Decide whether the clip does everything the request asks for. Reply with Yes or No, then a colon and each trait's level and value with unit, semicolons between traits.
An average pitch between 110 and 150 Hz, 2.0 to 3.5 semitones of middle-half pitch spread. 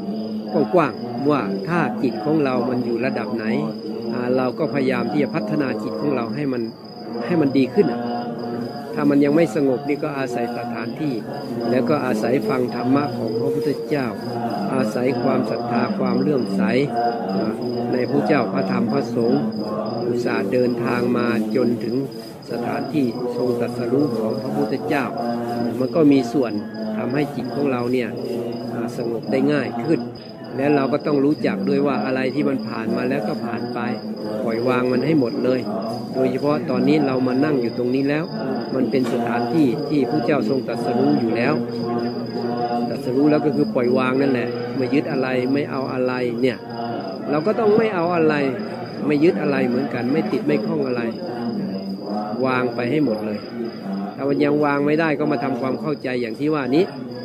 Yes: low, 125 Hz; average, 2.9 semitones